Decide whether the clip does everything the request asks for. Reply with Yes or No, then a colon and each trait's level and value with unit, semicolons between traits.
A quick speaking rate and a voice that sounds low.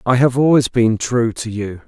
Yes: fast, 225 wpm; low, 120 Hz